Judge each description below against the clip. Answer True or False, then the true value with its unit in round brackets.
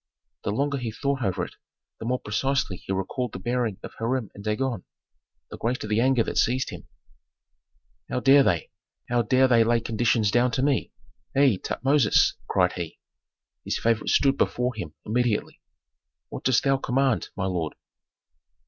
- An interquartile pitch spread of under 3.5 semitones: False (3.8 semitones)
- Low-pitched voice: True (120 Hz)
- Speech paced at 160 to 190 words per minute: True (165 wpm)